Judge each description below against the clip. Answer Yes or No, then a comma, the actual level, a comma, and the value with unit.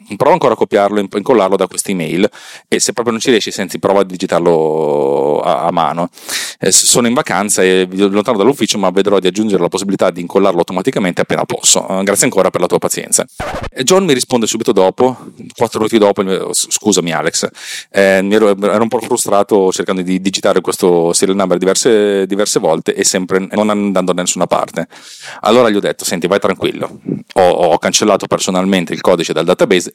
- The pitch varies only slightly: Yes, narrow, 2.3 semitones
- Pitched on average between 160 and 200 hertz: No, low, 100 Hz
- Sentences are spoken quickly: Yes, fast, 190 wpm